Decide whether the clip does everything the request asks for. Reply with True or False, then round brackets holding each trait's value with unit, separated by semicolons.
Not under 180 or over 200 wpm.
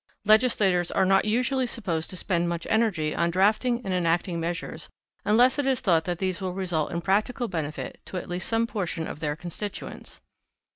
True (185 wpm)